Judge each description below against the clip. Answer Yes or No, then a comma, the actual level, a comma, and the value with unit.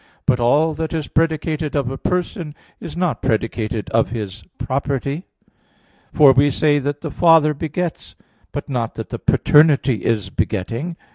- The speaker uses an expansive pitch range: No, average, 4.6 semitones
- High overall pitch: No, medium, 145 Hz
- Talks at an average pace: Yes, average, 150 wpm